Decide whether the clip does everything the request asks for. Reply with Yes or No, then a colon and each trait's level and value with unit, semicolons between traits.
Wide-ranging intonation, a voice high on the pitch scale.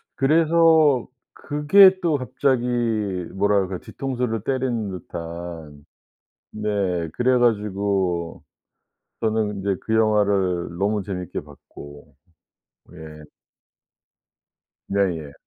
No: wide, 6.3 semitones; low, 100 Hz